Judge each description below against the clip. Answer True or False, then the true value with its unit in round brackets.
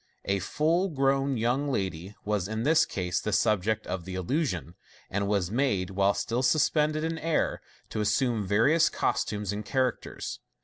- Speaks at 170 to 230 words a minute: False (160 wpm)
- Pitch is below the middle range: True (110 Hz)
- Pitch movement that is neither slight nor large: False (6.0 semitones)